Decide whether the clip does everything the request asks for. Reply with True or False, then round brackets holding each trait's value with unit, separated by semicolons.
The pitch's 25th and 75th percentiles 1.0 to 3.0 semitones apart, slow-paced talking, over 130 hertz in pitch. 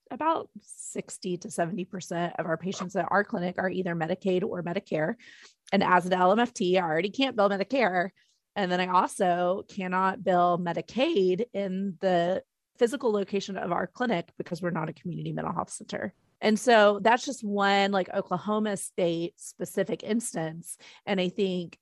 False (2.7 semitones; 160 wpm; 190 Hz)